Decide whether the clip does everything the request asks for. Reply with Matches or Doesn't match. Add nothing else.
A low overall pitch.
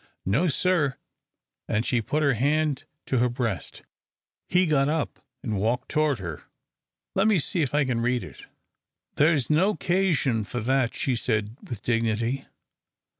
Matches